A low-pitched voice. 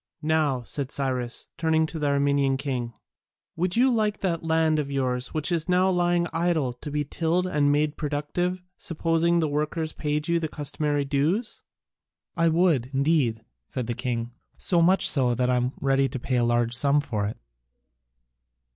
No: medium, 150 Hz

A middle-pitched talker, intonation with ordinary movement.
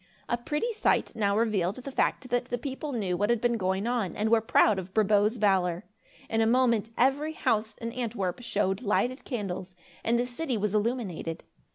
No: high, 225 Hz; average, 3.5 semitones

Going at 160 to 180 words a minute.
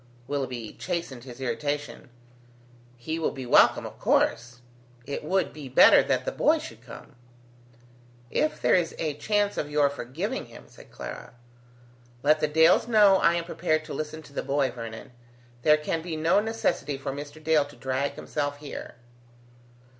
Yes: average, 165 wpm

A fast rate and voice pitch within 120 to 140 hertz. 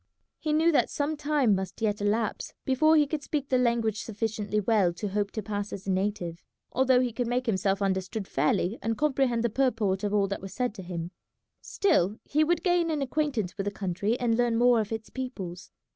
No: fast, 210 wpm; high, 225 Hz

